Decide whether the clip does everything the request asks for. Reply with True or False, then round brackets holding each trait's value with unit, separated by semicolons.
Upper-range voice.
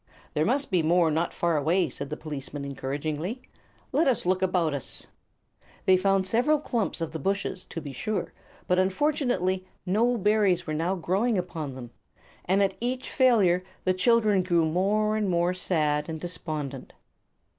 False (180 Hz)